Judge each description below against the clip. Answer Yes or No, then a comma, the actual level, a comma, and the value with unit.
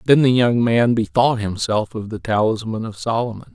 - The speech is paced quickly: No, average, 185 wpm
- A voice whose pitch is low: Yes, low, 115 Hz